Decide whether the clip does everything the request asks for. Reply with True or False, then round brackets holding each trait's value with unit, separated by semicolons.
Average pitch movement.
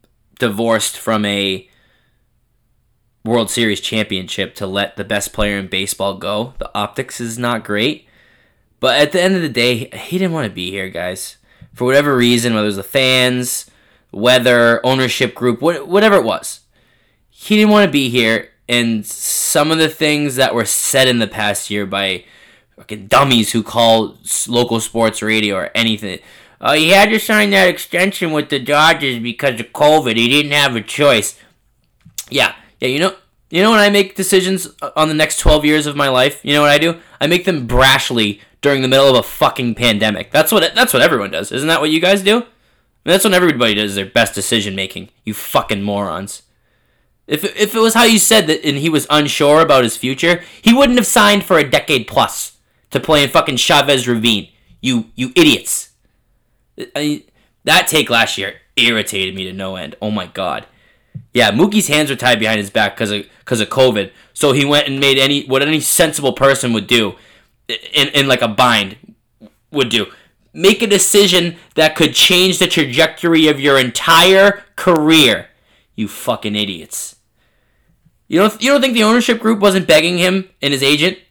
False (6.2 semitones)